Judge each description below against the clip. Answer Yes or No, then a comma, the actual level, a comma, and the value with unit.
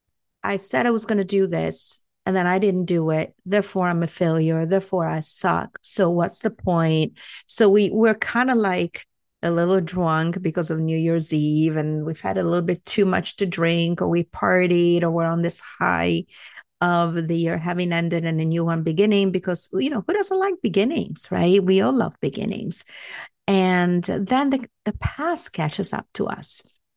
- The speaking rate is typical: Yes, average, 195 wpm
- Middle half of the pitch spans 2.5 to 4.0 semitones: Yes, average, 3.1 semitones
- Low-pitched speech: No, medium, 175 Hz